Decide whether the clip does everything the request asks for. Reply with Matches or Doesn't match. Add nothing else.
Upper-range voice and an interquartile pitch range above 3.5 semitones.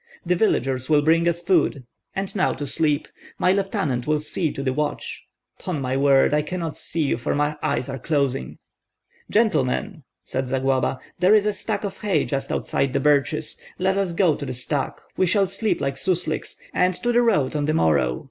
Doesn't match